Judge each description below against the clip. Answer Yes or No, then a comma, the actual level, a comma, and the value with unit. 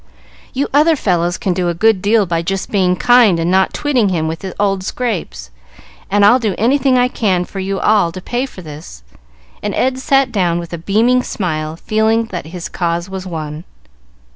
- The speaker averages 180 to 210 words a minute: Yes, average, 190 wpm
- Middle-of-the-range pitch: No, high, 195 Hz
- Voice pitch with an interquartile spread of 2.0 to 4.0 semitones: No, average, 4.9 semitones